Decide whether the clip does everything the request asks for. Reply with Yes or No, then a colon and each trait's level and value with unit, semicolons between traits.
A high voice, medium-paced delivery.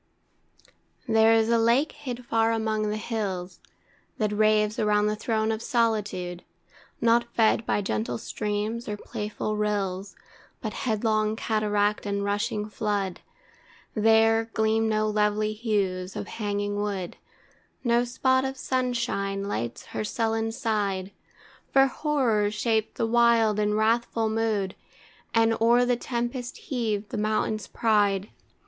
No: high, 215 Hz; slow, 130 wpm